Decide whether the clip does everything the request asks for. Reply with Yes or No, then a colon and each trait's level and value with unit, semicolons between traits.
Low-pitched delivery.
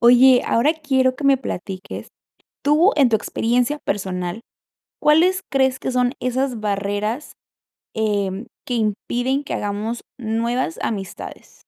No: high, 245 Hz